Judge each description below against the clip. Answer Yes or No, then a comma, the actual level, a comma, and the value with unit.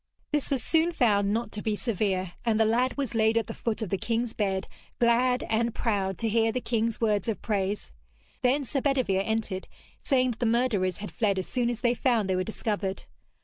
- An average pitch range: Yes, average, 3.1 semitones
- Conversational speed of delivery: No, fast, 215 wpm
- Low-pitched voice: No, high, 225 Hz